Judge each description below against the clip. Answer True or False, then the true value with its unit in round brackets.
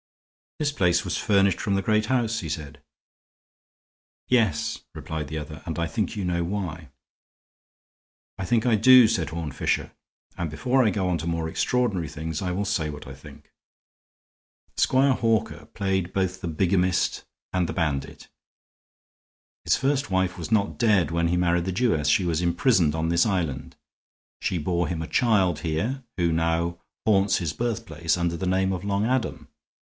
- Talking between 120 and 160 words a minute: False (170 wpm)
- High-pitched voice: False (90 Hz)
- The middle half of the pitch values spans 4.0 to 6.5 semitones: True (4.4 semitones)